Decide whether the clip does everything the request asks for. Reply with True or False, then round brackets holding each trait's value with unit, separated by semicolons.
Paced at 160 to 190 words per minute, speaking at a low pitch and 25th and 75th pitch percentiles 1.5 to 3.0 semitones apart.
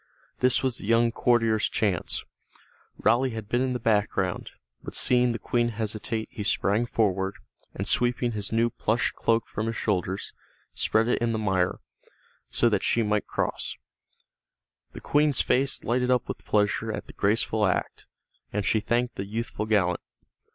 True (165 wpm; 115 Hz; 2.4 semitones)